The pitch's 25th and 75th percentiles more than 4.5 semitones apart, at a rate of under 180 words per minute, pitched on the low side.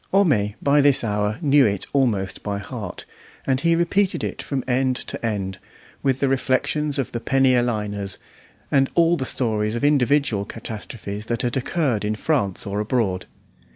Yes: average, 5.0 semitones; average, 170 wpm; low, 125 Hz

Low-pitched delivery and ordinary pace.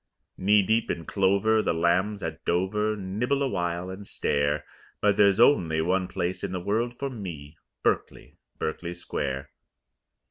Yes: very low, 95 Hz; average, 145 wpm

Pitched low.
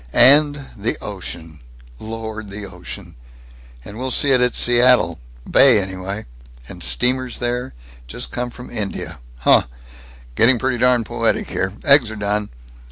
Yes: low, 115 Hz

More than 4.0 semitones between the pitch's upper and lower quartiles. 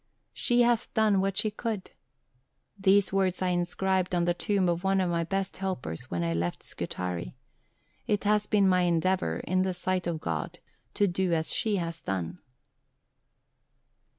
No: narrow, 2.6 semitones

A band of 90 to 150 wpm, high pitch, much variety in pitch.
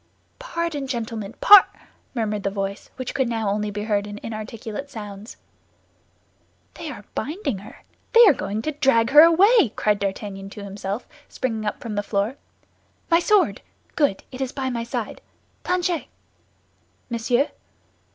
Yes: average, 145 wpm; high, 230 Hz; wide, 5.7 semitones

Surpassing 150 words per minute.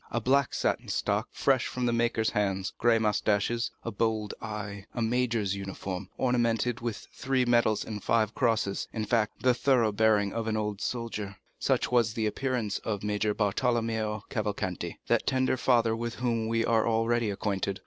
Yes: average, 160 wpm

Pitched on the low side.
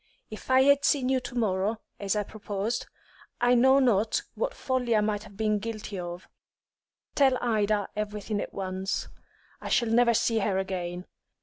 No: high, 215 Hz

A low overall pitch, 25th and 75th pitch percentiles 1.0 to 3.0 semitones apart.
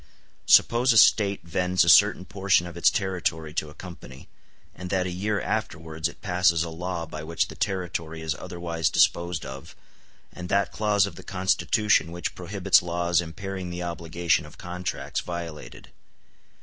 Yes: very low, 90 Hz; narrow, 2.4 semitones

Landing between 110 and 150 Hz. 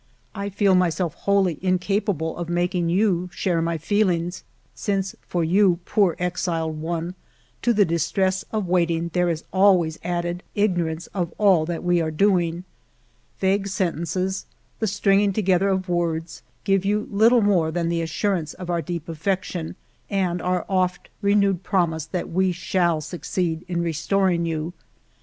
No: medium, 180 Hz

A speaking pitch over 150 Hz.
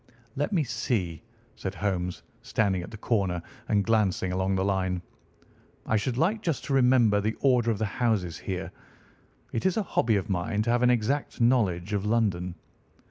No: low, 105 Hz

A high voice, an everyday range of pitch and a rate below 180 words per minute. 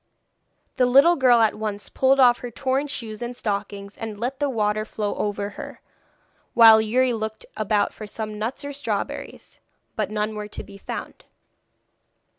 Yes: high, 220 Hz; average, 3.1 semitones; average, 165 wpm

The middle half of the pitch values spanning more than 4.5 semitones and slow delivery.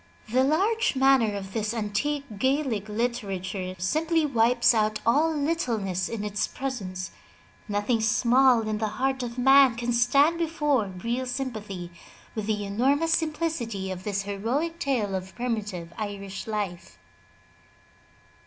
Yes: average, 5.0 semitones; slow, 130 wpm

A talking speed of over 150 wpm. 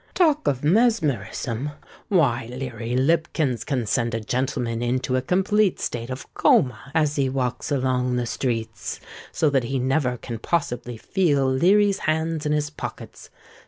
No: average, 145 wpm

